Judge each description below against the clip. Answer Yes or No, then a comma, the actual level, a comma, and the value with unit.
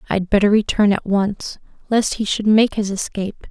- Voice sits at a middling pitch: No, high, 205 Hz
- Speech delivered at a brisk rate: No, average, 190 wpm